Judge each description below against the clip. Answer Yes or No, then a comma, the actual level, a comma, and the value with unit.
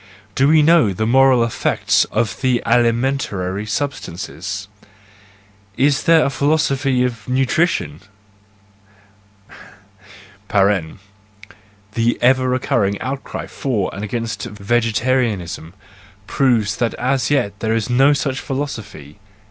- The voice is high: No, low, 115 Hz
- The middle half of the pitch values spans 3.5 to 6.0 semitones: Yes, average, 4.9 semitones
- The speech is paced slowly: Yes, slow, 100 wpm